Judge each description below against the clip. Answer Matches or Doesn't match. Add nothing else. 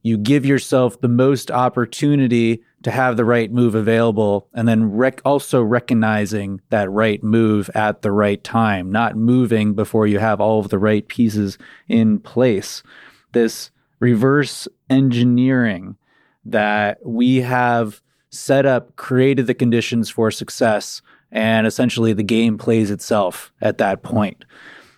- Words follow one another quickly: Doesn't match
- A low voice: Matches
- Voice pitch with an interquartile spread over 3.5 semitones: Doesn't match